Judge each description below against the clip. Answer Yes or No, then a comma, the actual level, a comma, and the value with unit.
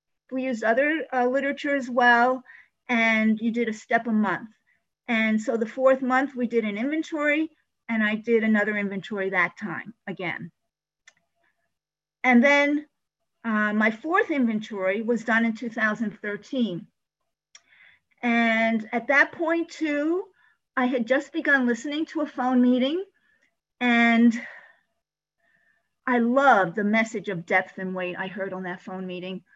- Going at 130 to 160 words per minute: Yes, average, 140 wpm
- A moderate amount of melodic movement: Yes, average, 4.1 semitones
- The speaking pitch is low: No, high, 235 Hz